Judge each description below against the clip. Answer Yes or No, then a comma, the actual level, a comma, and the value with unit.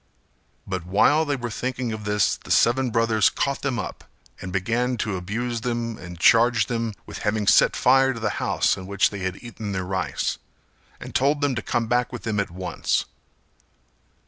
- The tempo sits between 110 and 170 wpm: No, average, 190 wpm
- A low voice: Yes, low, 115 Hz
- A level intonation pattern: No, average, 3.7 semitones